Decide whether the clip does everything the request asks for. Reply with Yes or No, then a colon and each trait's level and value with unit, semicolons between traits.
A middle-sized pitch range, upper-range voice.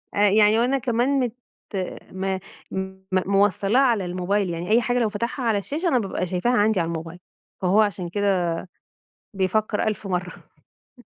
Yes: average, 3.6 semitones; high, 205 Hz